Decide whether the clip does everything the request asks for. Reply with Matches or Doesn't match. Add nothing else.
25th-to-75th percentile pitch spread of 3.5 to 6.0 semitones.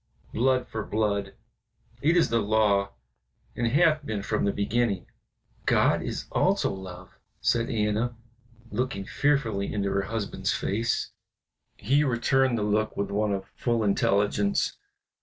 Doesn't match